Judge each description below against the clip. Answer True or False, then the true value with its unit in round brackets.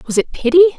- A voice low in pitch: False (300 Hz)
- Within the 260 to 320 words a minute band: False (230 wpm)